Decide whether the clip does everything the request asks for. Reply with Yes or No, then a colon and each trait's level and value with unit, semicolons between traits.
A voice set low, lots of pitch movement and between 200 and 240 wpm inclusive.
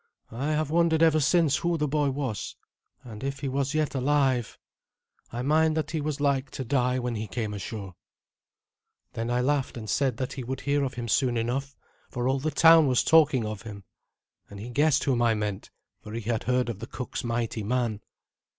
No: low, 130 Hz; average, 3.8 semitones; fast, 205 wpm